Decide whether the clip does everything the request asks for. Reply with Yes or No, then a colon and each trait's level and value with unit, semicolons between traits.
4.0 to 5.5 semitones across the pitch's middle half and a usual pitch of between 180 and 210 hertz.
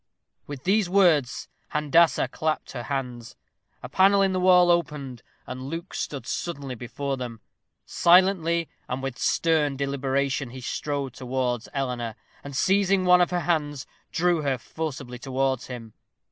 No: average, 4.8 semitones; medium, 140 Hz